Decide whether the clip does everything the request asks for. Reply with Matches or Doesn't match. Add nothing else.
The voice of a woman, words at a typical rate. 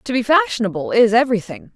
Matches